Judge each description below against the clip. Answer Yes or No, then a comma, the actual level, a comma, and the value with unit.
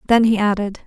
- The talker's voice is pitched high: Yes, high, 210 Hz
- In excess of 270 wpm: No, fast, 210 wpm